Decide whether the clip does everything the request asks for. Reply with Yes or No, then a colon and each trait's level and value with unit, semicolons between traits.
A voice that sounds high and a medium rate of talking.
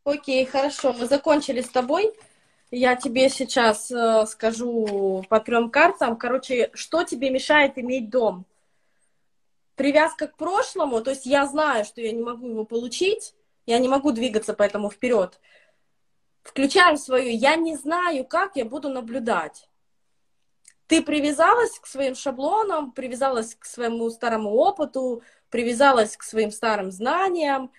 Yes: very high, 260 Hz; average, 135 wpm